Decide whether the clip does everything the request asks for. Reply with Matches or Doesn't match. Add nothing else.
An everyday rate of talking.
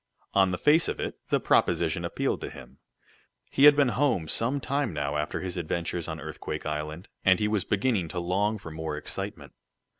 Matches